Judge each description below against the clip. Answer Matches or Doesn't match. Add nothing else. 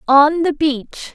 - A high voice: Matches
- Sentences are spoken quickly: Doesn't match